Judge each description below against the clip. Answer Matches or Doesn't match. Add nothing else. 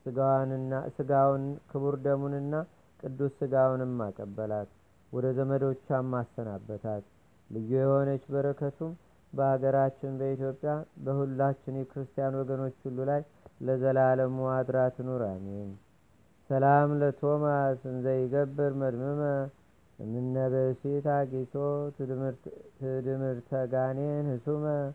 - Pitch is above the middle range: Doesn't match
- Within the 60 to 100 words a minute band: Matches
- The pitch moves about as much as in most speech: Doesn't match